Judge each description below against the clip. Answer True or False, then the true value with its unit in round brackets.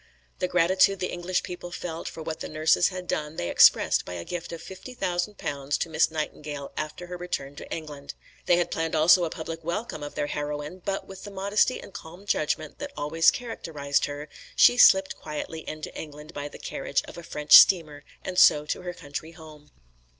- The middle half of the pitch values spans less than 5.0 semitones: True (3.2 semitones)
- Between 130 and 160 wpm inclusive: False (200 wpm)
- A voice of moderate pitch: True (165 Hz)